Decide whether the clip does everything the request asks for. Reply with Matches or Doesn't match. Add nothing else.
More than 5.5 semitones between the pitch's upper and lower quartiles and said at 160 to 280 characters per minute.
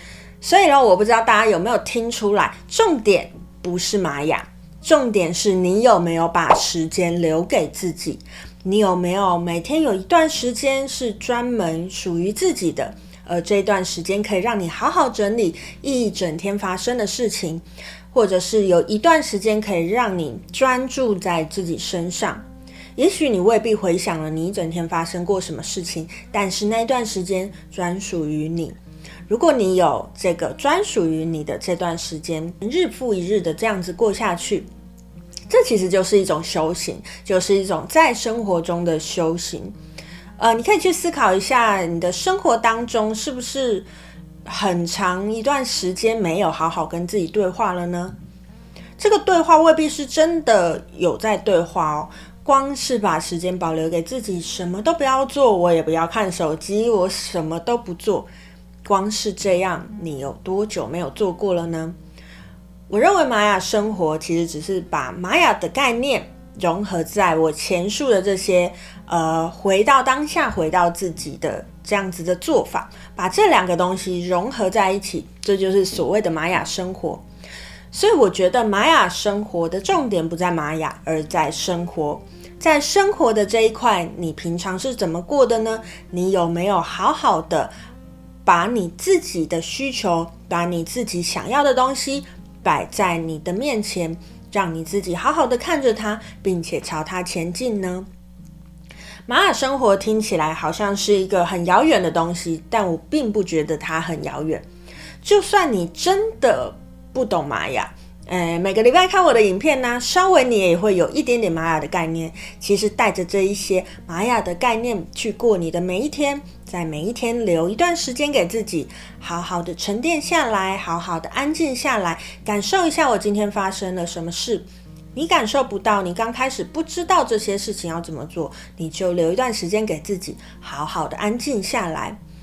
Doesn't match